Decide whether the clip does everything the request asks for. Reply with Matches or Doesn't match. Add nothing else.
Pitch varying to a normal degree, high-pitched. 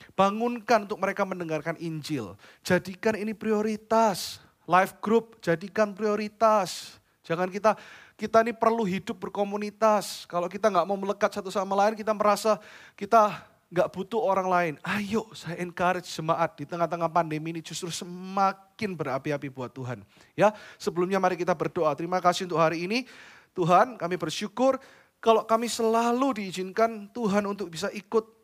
Matches